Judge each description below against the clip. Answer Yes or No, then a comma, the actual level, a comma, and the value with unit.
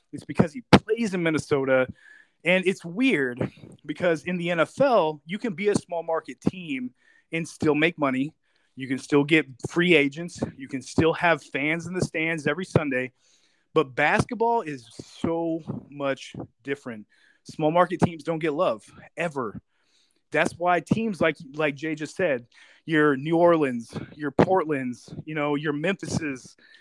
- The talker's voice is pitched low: No, medium, 160 Hz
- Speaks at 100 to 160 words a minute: Yes, average, 155 wpm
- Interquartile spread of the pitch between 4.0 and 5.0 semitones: No, average, 3.6 semitones